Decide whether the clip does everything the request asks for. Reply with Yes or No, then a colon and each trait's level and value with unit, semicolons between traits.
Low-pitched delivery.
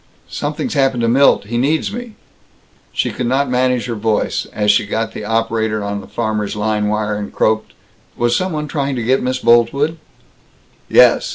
Yes: low, 120 Hz